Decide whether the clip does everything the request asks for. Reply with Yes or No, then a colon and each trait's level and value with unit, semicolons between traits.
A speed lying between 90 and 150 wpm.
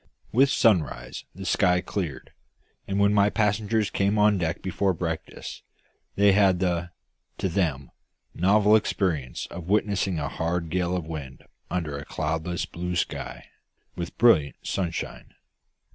Yes: slow, 135 wpm